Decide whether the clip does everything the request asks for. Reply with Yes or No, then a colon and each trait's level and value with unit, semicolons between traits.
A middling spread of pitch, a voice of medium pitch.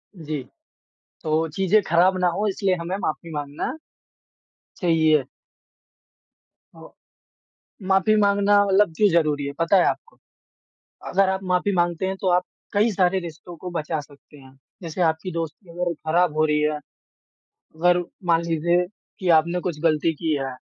Yes: average, 3.2 semitones; medium, 170 Hz